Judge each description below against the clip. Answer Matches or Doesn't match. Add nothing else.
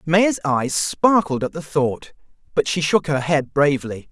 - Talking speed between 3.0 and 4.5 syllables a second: Matches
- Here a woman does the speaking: Doesn't match